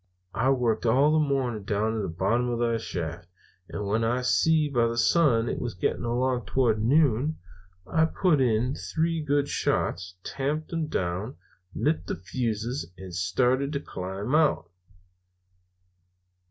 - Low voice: Yes, low, 120 Hz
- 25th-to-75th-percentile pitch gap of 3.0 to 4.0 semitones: No, average, 4.9 semitones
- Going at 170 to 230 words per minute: No, average, 155 wpm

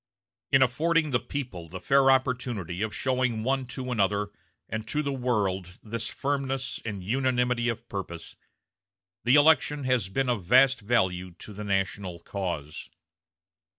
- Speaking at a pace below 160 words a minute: Yes, average, 145 wpm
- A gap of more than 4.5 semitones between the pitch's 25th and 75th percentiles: Yes, average, 5.1 semitones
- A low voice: Yes, low, 120 Hz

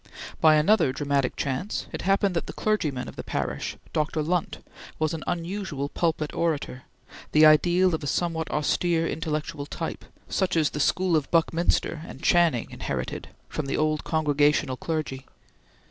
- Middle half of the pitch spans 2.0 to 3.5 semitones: Yes, average, 2.7 semitones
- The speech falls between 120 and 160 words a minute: Yes, average, 155 wpm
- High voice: No, medium, 155 Hz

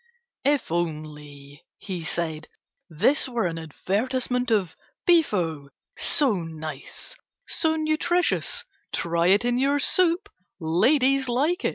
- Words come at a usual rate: No, slow, 110 wpm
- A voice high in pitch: Yes, high, 205 Hz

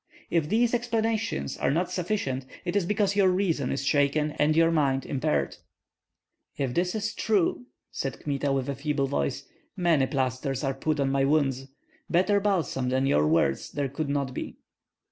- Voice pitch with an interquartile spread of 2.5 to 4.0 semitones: No, average, 5.2 semitones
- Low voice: No, medium, 145 Hz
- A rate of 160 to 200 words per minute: Yes, average, 170 wpm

